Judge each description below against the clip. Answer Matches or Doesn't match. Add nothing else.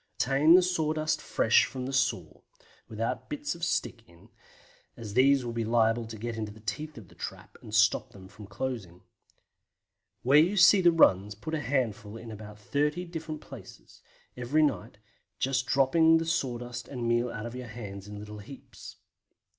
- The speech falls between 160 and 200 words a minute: Matches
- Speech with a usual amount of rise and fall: Doesn't match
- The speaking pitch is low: Matches